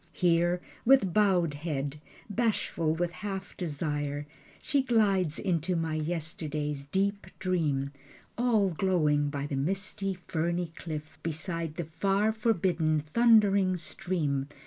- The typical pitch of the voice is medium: Yes, medium, 170 Hz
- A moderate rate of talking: No, slow, 115 wpm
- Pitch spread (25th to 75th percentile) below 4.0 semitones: No, average, 4.3 semitones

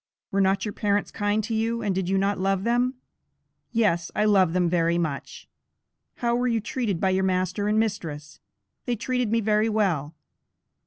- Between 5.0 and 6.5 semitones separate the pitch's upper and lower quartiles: No, average, 3.4 semitones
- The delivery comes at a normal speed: Yes, average, 180 wpm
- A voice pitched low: No, high, 205 Hz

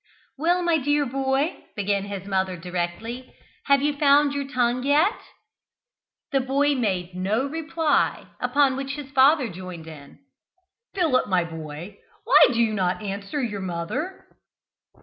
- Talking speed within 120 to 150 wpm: Yes, average, 140 wpm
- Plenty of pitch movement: Yes, wide, 7.2 semitones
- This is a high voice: Yes, very high, 250 Hz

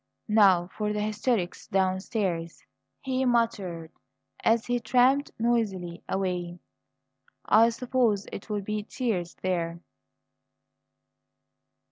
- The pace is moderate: No, slow, 90 wpm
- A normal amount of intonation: Yes, average, 4.3 semitones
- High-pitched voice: Yes, high, 210 Hz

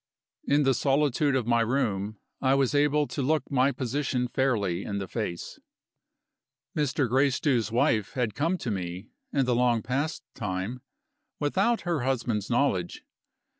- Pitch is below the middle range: Yes, low, 125 Hz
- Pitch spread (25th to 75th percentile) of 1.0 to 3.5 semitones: No, average, 4.3 semitones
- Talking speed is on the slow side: No, average, 145 wpm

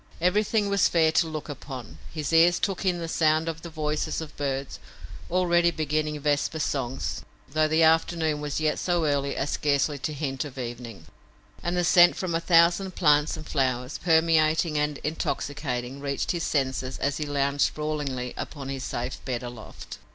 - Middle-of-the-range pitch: Yes, medium, 150 Hz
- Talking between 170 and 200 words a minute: Yes, average, 175 wpm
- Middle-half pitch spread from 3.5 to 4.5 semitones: No, average, 3.0 semitones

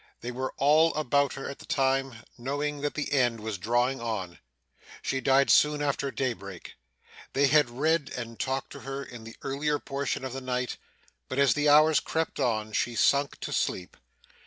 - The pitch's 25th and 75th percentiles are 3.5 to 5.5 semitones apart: No, average, 3.1 semitones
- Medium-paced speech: Yes, average, 185 wpm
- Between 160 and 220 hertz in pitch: No, low, 135 Hz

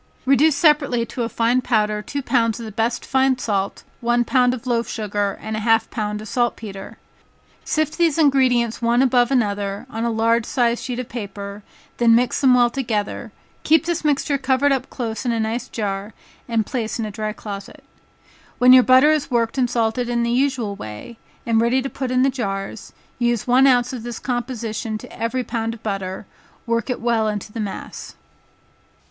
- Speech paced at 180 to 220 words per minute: Yes, average, 190 wpm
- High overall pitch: Yes, high, 235 Hz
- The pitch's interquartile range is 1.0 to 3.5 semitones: Yes, average, 2.7 semitones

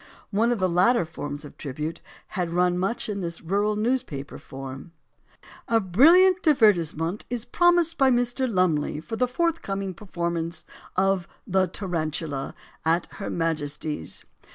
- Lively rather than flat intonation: Yes, wide, 6.1 semitones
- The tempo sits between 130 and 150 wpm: Yes, average, 140 wpm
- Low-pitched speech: No, medium, 185 Hz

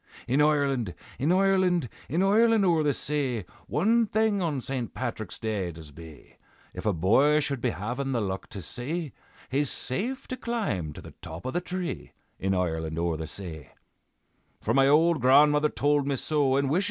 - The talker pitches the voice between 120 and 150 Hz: Yes, medium, 140 Hz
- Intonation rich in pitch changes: Yes, wide, 9.0 semitones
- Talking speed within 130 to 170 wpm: No, average, 180 wpm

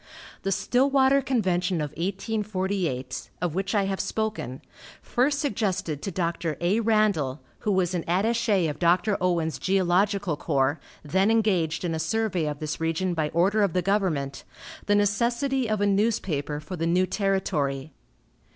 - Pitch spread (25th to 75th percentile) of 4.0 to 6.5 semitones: Yes, average, 4.6 semitones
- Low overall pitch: No, medium, 185 Hz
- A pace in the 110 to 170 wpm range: Yes, average, 150 wpm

